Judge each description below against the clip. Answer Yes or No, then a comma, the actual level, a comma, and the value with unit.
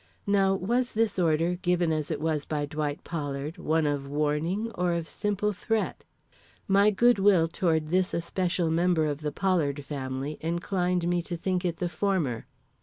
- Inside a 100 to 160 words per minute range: No, average, 170 wpm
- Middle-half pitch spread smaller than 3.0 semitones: No, average, 3.8 semitones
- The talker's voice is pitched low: No, medium, 170 Hz